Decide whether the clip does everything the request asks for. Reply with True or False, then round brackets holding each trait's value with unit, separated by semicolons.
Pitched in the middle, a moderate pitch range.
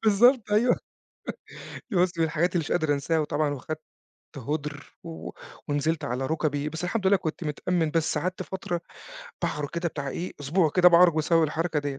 True (160 Hz; 3.2 semitones)